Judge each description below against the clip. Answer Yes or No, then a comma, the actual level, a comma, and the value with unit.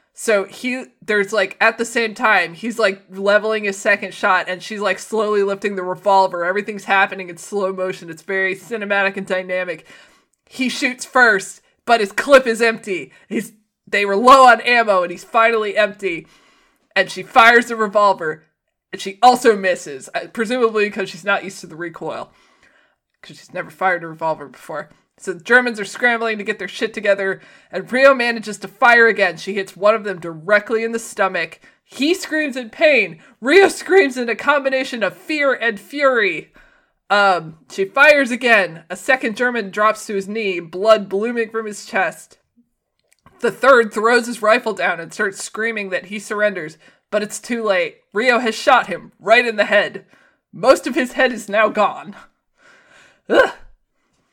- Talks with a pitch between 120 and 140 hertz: No, high, 215 Hz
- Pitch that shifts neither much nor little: Yes, average, 3.9 semitones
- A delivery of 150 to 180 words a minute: Yes, average, 175 wpm